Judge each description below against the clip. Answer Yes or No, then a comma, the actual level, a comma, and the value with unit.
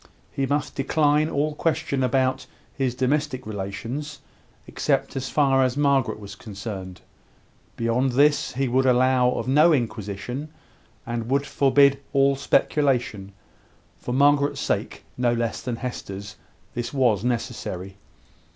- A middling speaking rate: No, slow, 125 wpm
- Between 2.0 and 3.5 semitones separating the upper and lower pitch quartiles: Yes, average, 3.2 semitones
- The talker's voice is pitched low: Yes, low, 130 Hz